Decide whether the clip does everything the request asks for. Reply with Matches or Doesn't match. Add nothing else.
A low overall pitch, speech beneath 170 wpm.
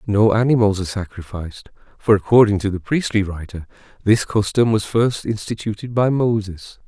Matches